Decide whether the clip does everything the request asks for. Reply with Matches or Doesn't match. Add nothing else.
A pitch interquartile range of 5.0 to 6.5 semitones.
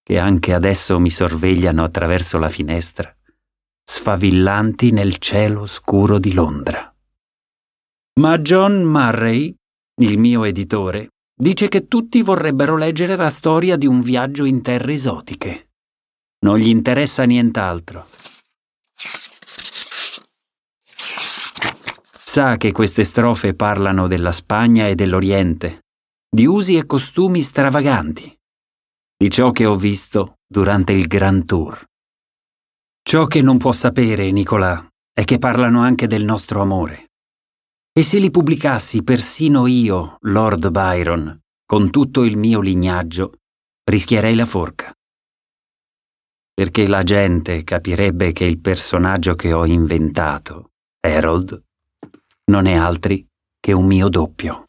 Matches